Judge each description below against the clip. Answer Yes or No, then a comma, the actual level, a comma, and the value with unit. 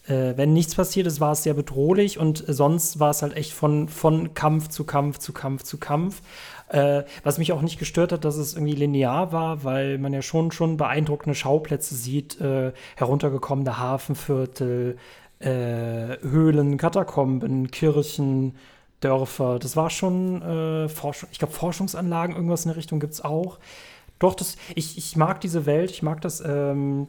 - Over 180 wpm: No, average, 170 wpm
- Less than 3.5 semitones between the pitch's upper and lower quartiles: Yes, average, 2.8 semitones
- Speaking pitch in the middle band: Yes, medium, 150 Hz